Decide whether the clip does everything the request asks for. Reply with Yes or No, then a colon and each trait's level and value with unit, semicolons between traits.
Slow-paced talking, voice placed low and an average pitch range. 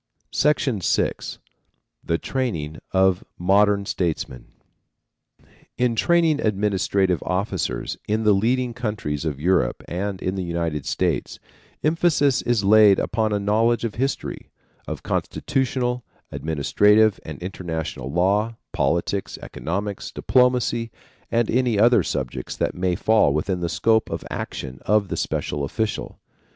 Yes: slow, 120 wpm; low, 100 Hz; average, 5.0 semitones